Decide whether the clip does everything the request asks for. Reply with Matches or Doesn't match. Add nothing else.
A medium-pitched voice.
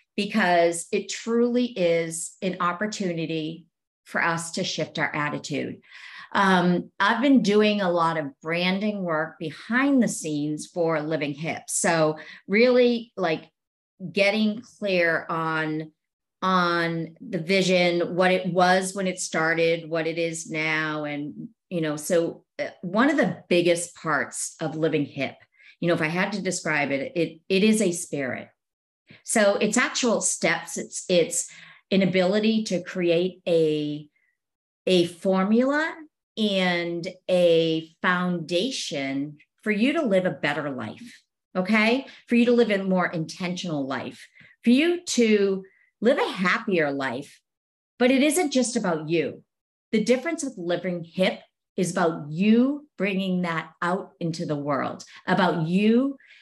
Matches